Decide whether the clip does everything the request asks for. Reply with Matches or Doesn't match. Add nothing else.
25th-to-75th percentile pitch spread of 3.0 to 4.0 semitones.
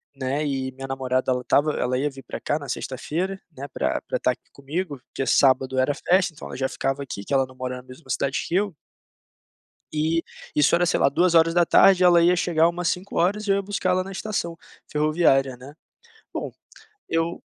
Doesn't match